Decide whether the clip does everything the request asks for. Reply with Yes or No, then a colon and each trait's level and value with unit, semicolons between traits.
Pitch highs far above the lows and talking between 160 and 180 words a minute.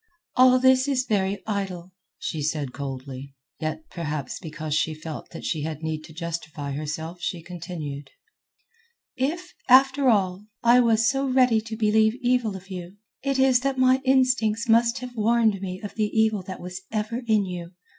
Yes: wide, 7.2 semitones; average, 170 wpm